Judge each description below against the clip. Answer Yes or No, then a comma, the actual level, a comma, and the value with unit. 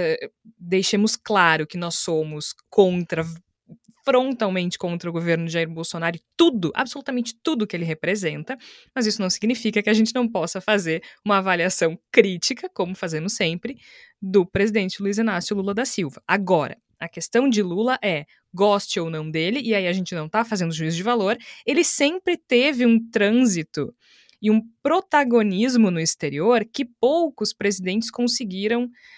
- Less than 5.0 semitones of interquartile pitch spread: No, wide, 5.4 semitones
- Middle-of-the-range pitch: No, high, 205 Hz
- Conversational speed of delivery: Yes, average, 160 wpm